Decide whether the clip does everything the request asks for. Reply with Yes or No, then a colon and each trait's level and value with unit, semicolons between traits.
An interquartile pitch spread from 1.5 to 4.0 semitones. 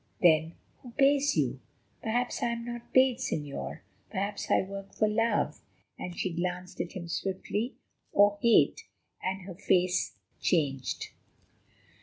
No: average, 4.7 semitones